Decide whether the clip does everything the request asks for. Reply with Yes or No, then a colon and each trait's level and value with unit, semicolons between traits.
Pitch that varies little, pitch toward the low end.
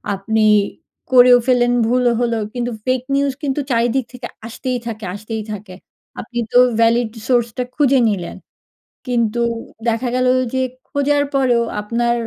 No: narrow, 1.9 semitones; high, 240 Hz